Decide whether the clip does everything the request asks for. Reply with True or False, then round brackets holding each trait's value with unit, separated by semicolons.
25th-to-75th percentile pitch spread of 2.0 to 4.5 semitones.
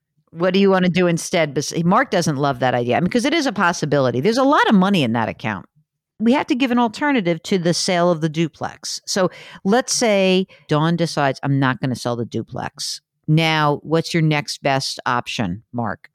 False (5.0 semitones)